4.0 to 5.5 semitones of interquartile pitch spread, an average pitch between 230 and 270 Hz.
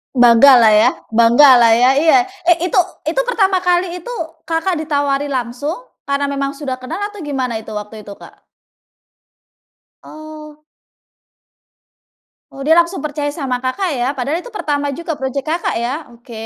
No: average, 4.7 semitones; very high, 285 Hz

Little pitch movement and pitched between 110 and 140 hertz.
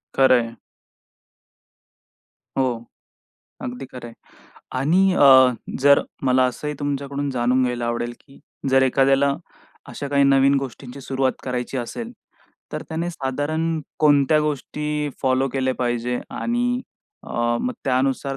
Yes: narrow, 2.3 semitones; low, 135 Hz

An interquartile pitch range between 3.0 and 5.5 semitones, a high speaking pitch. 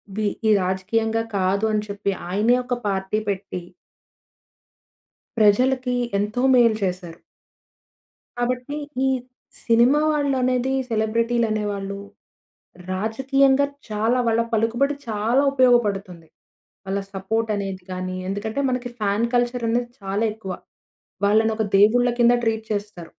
Yes: average, 3.5 semitones; high, 220 Hz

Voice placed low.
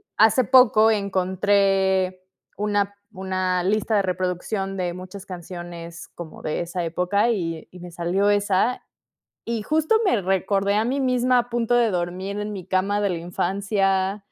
No: high, 195 Hz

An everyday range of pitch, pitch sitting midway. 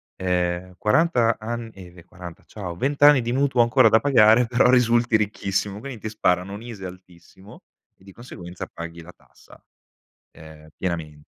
No: average, 4.8 semitones; low, 105 Hz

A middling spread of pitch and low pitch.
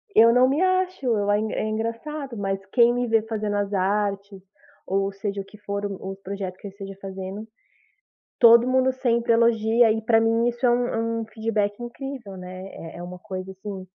No: average, 3.2 semitones; high, 215 Hz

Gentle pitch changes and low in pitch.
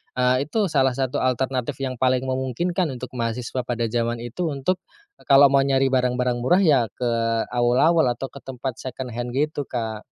Yes: narrow, 2.0 semitones; low, 130 Hz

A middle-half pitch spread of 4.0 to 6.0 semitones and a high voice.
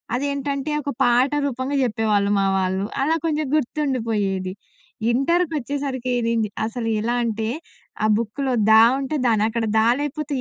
Yes: average, 4.3 semitones; very high, 250 Hz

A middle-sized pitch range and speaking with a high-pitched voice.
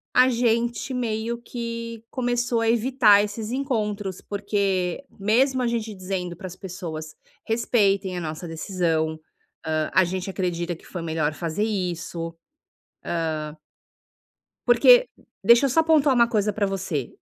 Yes: average, 5.0 semitones; high, 205 Hz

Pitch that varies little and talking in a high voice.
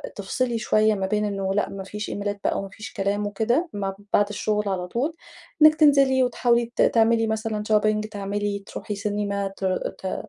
Yes: narrow, 2.3 semitones; high, 210 Hz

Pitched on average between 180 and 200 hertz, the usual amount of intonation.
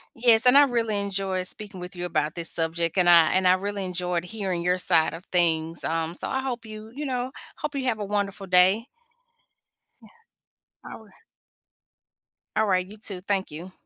Yes: high, 190 Hz; average, 3.6 semitones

